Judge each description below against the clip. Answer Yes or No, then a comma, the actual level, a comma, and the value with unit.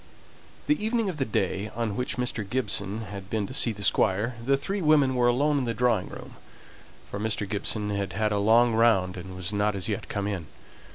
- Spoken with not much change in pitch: No, average, 3.9 semitones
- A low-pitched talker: Yes, low, 110 Hz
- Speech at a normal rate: No, fast, 215 wpm